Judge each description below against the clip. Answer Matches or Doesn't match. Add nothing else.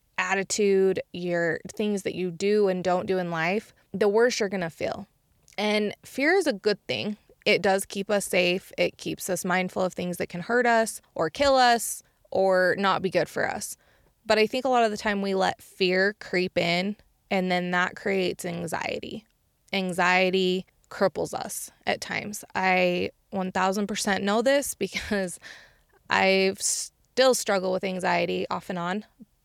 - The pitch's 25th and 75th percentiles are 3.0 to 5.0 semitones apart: Doesn't match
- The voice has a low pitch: Doesn't match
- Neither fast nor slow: Matches